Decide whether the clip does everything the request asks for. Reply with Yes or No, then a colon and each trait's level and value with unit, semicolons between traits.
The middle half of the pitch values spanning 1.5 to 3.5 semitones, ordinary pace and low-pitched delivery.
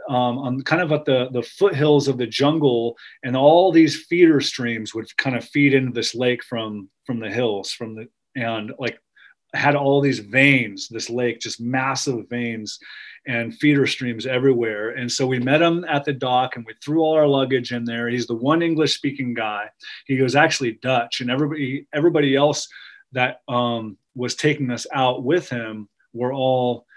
Yes: average, 3.2 semitones; average, 185 wpm; low, 130 Hz